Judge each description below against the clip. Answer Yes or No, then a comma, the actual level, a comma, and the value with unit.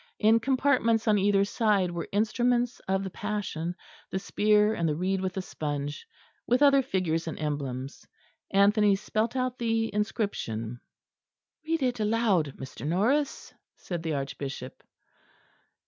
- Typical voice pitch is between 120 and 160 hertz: No, high, 200 Hz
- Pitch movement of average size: No, wide, 5.7 semitones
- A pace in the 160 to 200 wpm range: No, slow, 135 wpm